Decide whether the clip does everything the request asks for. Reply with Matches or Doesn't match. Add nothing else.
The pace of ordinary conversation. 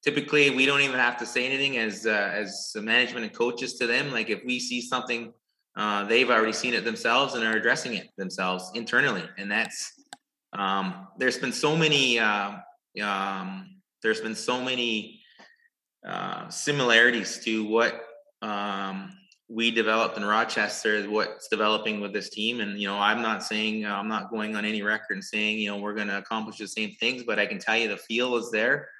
Matches